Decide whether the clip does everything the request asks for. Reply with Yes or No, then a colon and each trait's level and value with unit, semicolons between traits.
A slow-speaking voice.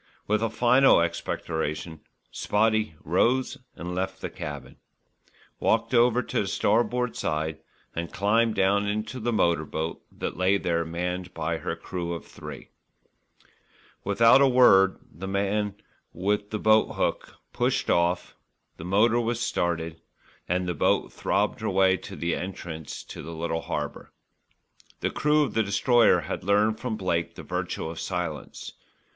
No: average, 150 wpm